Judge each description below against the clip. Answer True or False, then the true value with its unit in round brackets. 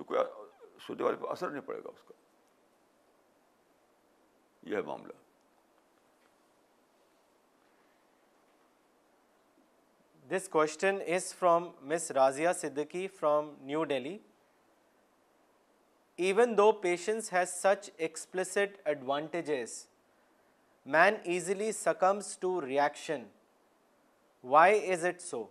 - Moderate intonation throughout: True (4.4 semitones)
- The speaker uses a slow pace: True (80 wpm)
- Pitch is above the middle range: False (180 Hz)